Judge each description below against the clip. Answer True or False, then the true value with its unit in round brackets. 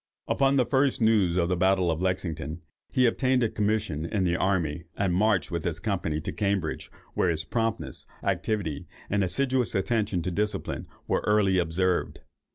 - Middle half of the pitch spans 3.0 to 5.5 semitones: True (4.2 semitones)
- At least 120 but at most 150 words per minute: False (165 wpm)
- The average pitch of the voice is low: True (95 Hz)